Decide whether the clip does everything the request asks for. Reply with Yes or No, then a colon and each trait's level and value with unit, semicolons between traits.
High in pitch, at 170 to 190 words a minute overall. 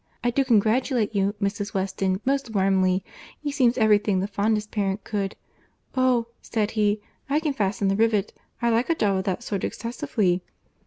Yes: high, 210 Hz; average, 175 wpm